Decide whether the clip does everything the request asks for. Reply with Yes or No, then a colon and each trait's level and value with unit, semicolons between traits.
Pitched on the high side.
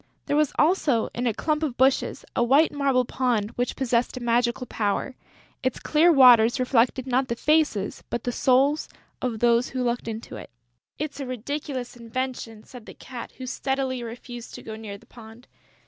Yes: very high, 250 Hz